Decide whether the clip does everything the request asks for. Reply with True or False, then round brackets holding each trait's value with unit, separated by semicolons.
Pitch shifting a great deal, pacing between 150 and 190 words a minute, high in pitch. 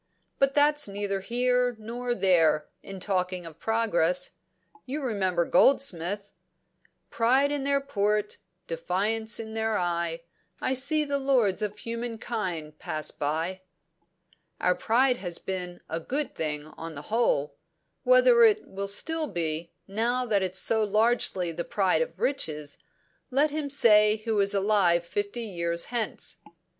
False (5.7 semitones; 140 wpm; 210 Hz)